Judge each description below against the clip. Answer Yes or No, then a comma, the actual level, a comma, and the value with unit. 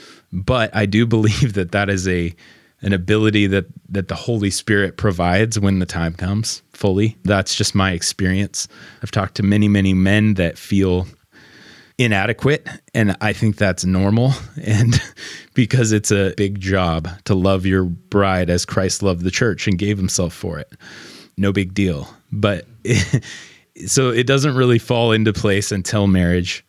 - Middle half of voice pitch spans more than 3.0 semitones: No, average, 2.7 semitones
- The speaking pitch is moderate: No, low, 100 Hz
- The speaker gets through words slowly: No, average, 165 wpm